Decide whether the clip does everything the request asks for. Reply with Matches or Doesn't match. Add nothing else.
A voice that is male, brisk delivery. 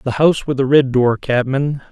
Matches